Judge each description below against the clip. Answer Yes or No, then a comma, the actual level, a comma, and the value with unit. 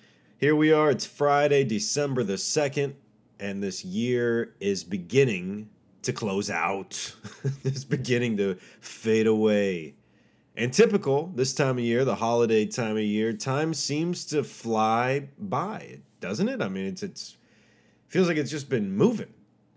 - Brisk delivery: No, average, 150 wpm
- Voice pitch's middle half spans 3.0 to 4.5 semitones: No, wide, 5.4 semitones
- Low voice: Yes, low, 130 Hz